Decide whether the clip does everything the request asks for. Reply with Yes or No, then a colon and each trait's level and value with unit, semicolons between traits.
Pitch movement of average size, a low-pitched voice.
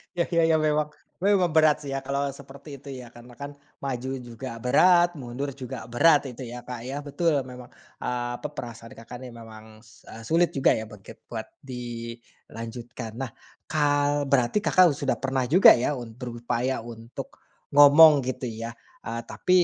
Yes: average, 3.5 semitones; low, 130 Hz